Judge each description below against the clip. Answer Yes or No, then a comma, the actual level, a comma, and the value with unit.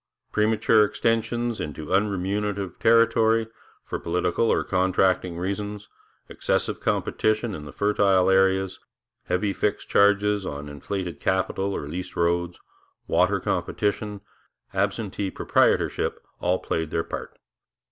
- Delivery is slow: Yes, slow, 110 wpm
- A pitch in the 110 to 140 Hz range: No, very low, 95 Hz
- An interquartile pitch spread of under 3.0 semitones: Yes, narrow, 2.6 semitones